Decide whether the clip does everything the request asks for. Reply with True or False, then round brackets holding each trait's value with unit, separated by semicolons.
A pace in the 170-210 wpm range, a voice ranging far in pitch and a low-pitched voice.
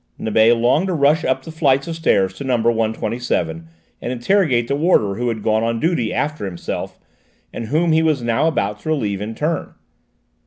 True (190 wpm; 6.0 semitones; 120 Hz)